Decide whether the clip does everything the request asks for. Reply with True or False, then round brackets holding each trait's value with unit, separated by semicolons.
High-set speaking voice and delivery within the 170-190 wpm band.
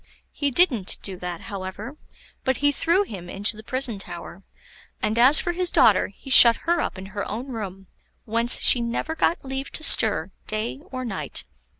True (230 Hz; 185 wpm)